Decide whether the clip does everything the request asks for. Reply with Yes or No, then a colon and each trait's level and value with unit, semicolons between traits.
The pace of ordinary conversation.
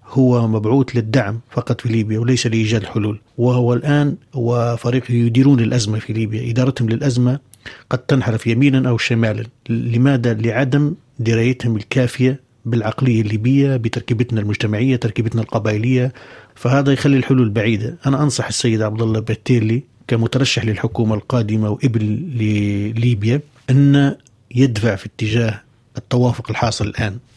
Yes: average, 120 wpm